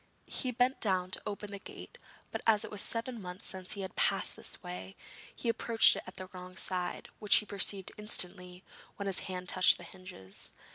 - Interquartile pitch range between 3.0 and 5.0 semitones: No, narrow, 2.5 semitones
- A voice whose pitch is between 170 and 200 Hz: Yes, high, 190 Hz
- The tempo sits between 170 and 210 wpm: Yes, average, 200 wpm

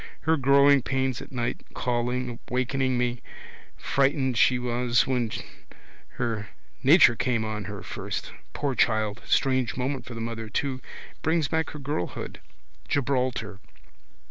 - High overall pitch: No, low, 125 Hz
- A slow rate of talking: Yes, slow, 130 wpm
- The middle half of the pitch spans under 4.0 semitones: Yes, narrow, 2.5 semitones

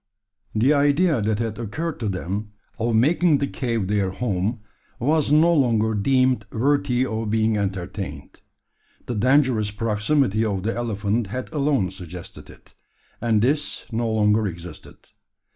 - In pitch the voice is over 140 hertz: No, low, 110 Hz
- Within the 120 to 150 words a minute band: Yes, average, 140 wpm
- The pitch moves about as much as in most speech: Yes, average, 4.2 semitones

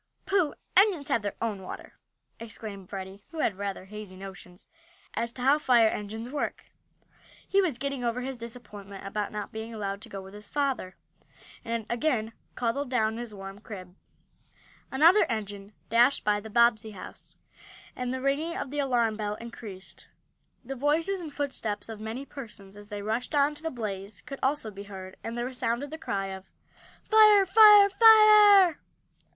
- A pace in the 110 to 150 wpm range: No, average, 175 wpm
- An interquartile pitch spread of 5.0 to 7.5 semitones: Yes, wide, 5.6 semitones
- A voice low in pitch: No, high, 230 Hz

